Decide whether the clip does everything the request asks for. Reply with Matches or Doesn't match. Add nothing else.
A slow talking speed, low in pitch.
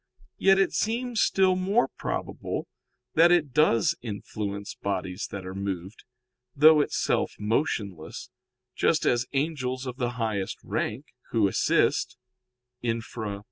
Matches